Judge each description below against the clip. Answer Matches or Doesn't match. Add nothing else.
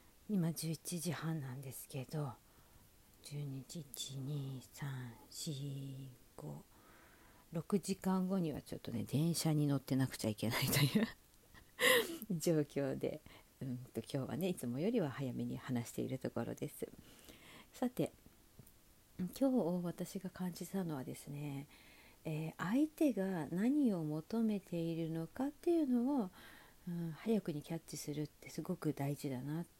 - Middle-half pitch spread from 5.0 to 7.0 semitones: Matches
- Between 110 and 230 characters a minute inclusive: Doesn't match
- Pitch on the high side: Doesn't match